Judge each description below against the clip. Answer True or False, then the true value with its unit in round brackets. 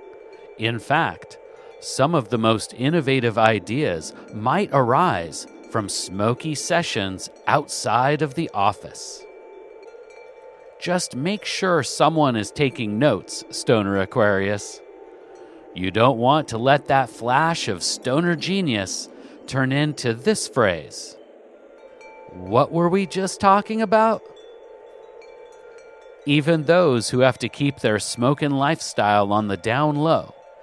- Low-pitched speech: False (170 Hz)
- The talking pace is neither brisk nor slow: False (115 wpm)